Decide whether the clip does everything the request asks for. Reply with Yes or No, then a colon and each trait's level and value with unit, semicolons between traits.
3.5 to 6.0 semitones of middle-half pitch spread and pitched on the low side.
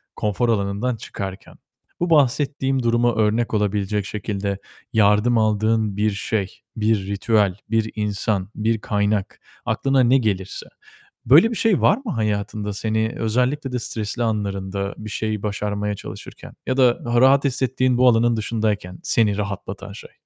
No: average, 2.8 semitones; low, 110 Hz